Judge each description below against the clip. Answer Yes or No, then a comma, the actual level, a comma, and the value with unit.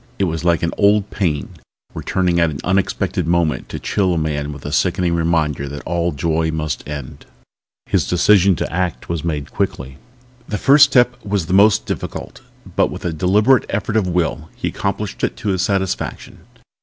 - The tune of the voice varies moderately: Yes, average, 3.9 semitones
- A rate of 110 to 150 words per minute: No, average, 180 wpm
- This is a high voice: No, very low, 85 Hz